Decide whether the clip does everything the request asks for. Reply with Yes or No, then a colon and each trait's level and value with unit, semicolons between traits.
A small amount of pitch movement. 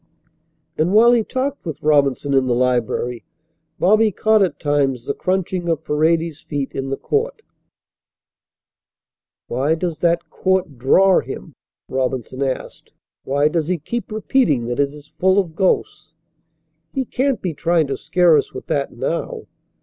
No: wide, 5.5 semitones